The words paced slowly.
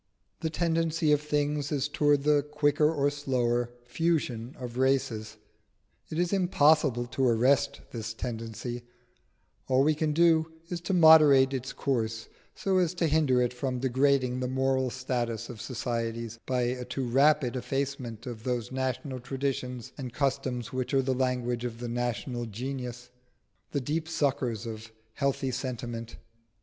No: average, 150 wpm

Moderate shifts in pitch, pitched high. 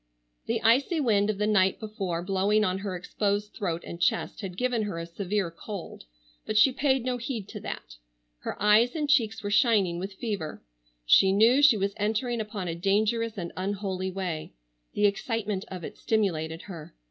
Yes: average, 3.1 semitones; high, 205 Hz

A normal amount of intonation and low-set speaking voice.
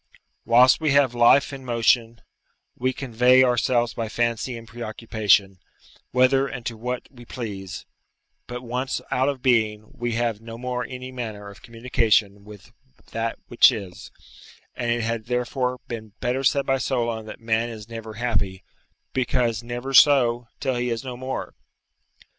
No: narrow, 2.0 semitones; low, 120 Hz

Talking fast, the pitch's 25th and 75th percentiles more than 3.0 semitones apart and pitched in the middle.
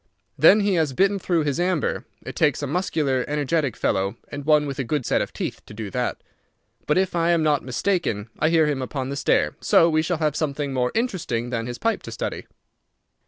Yes: fast, 215 wpm; average, 4.5 semitones; medium, 150 Hz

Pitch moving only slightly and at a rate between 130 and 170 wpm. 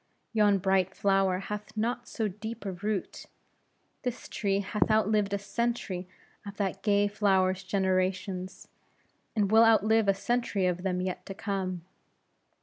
Yes: narrow, 2.3 semitones; average, 145 wpm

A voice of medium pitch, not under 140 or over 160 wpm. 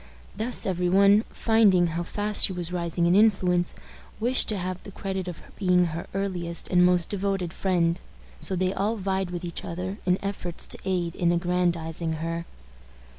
No: medium, 180 Hz; average, 175 wpm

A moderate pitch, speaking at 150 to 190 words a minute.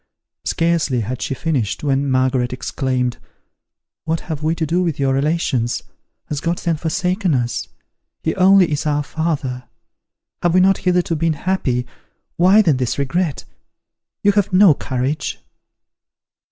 No: medium, 155 Hz; average, 140 wpm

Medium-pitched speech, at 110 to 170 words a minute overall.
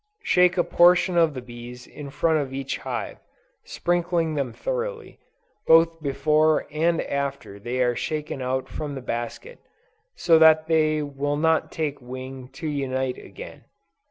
Yes: medium, 150 Hz; average, 150 wpm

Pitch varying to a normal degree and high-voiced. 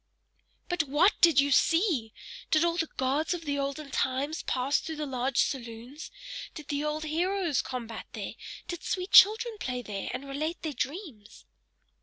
Yes: average, 4.2 semitones; very high, 295 Hz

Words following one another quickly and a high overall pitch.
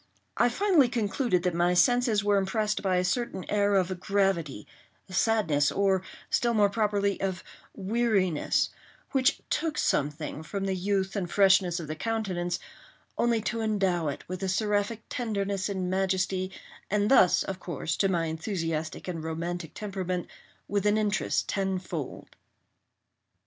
No: average, 145 wpm; high, 195 Hz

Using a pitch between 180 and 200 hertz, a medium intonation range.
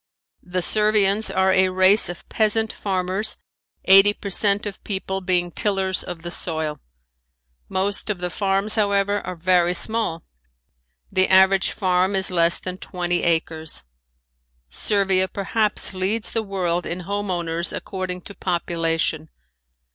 No: high, 190 Hz; narrow, 2.3 semitones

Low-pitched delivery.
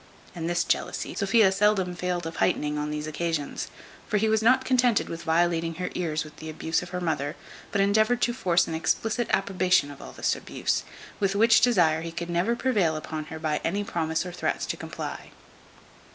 No: medium, 175 Hz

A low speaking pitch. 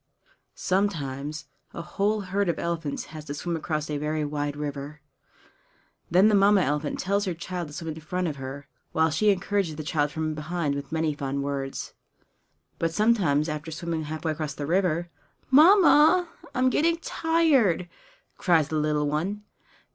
No: medium, 160 Hz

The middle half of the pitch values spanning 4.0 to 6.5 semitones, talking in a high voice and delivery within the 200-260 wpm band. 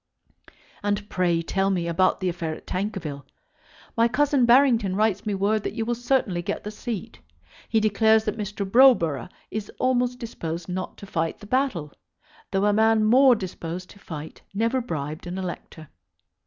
No: average, 4.5 semitones; high, 205 Hz; average, 170 wpm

